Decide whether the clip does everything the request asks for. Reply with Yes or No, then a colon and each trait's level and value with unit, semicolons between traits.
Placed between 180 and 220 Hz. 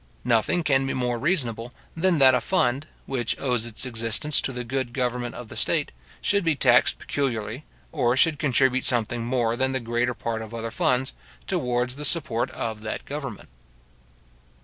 No: low, 125 Hz